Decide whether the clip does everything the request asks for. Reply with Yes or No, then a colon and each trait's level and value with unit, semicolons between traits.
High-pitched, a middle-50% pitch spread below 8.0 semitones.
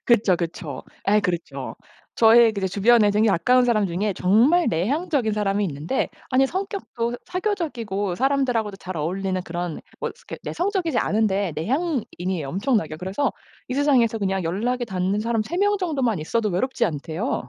Yes: high, 215 Hz; wide, 5.6 semitones